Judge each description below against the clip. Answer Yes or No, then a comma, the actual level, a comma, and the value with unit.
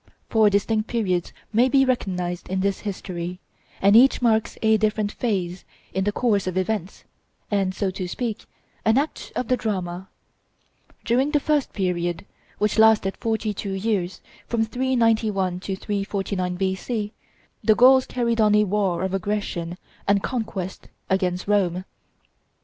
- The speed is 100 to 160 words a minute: Yes, average, 145 wpm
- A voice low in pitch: No, high, 205 Hz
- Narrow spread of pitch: No, average, 3.0 semitones